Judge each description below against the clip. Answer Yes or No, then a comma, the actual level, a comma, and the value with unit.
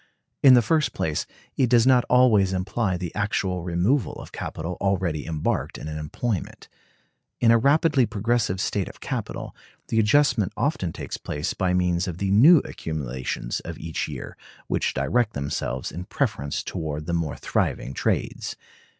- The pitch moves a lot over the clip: Yes, wide, 6.6 semitones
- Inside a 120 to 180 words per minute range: Yes, average, 160 wpm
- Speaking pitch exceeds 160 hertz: No, very low, 95 Hz